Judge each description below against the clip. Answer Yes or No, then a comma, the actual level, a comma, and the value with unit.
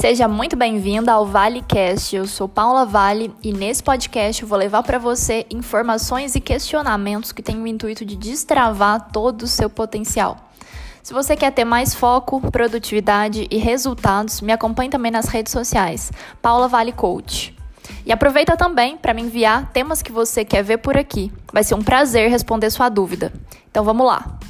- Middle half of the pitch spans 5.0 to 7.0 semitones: No, average, 2.9 semitones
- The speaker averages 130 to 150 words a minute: No, average, 175 wpm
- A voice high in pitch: Yes, high, 230 Hz